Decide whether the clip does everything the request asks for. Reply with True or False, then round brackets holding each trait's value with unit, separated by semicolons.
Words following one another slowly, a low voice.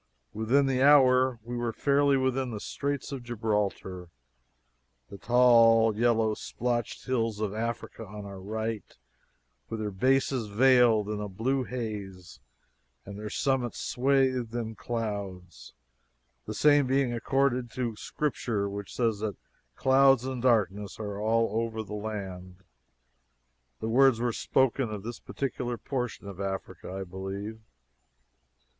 True (130 wpm; 115 Hz)